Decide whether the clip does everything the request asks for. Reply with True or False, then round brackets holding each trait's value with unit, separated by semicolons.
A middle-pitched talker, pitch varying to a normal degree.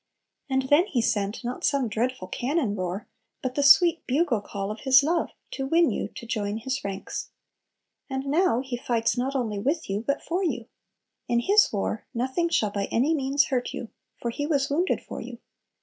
False (260 Hz; 4.3 semitones)